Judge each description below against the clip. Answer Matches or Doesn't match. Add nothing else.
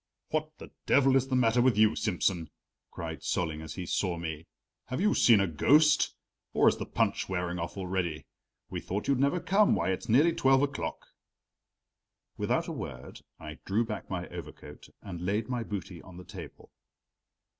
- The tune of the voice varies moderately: Doesn't match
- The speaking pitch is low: Matches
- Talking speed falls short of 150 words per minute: Doesn't match